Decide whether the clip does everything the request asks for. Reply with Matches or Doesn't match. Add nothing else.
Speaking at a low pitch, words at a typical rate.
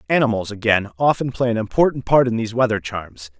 Matches